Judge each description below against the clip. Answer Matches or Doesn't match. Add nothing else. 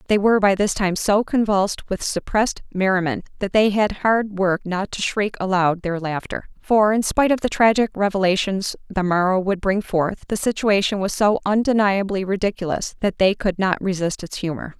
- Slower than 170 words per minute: Doesn't match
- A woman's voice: Matches